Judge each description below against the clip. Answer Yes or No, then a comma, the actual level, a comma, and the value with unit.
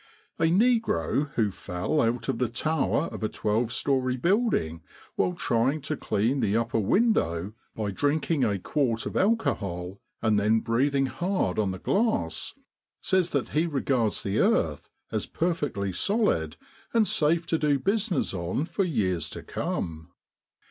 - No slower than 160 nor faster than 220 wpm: No, average, 150 wpm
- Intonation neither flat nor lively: No, wide, 8.3 semitones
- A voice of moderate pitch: No, low, 130 Hz